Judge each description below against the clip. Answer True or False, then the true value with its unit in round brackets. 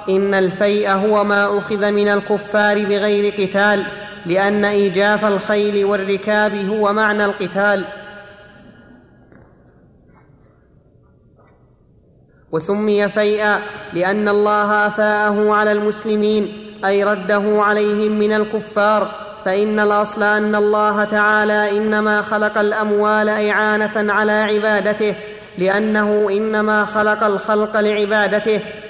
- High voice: True (210 Hz)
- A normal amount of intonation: False (0.6 semitones)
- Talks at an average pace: True (90 wpm)